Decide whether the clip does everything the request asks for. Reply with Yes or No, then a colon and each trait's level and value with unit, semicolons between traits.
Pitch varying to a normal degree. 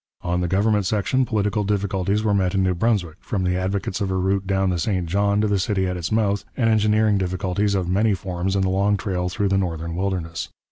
No: narrow, 2.0 semitones